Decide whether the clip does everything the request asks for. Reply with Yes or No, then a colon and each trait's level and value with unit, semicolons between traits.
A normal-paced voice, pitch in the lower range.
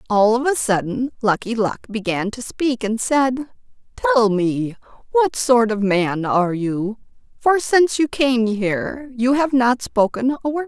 No: average, 170 wpm; high, 240 Hz